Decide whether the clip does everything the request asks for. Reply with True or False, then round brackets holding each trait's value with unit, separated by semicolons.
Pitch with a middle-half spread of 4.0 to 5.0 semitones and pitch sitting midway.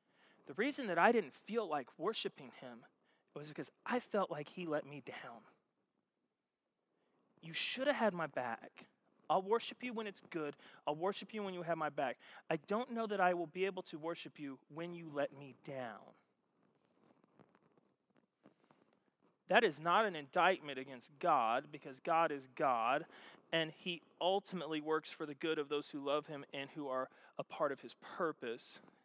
True (4.7 semitones; 165 Hz)